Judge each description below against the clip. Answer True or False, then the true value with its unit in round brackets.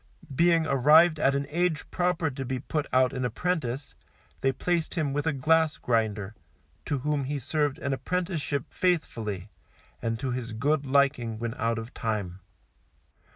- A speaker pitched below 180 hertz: True (140 Hz)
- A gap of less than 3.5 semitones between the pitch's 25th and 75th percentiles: False (4.5 semitones)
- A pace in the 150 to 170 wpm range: True (155 wpm)